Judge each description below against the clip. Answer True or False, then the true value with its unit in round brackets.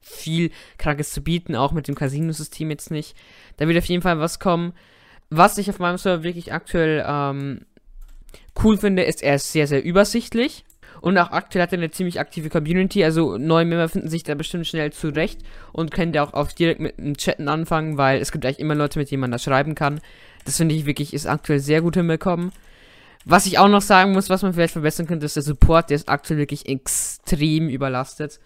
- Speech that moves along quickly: True (215 wpm)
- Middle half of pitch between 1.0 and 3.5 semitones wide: True (2.9 semitones)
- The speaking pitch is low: False (160 Hz)